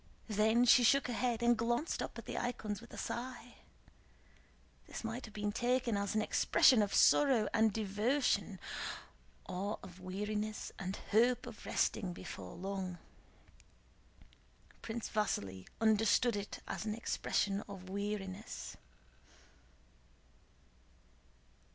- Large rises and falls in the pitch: No, average, 3.0 semitones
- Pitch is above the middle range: Yes, high, 215 Hz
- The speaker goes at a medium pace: No, slow, 120 wpm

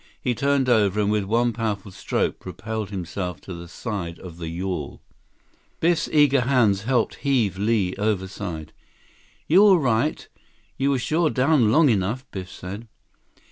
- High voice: No, low, 110 Hz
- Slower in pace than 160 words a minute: Yes, average, 150 wpm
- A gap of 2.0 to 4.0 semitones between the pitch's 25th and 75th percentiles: No, wide, 5.6 semitones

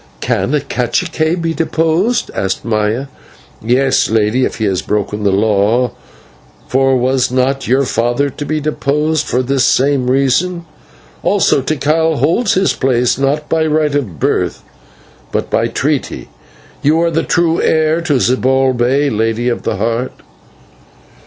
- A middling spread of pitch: Yes, average, 4.4 semitones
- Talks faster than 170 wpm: No, average, 145 wpm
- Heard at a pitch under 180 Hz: Yes, low, 135 Hz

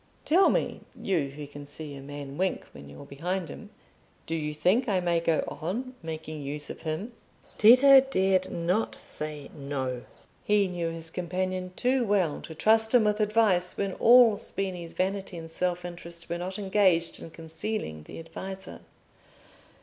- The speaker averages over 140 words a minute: Yes, average, 165 wpm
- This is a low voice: No, medium, 175 Hz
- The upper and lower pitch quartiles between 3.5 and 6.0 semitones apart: Yes, average, 4.2 semitones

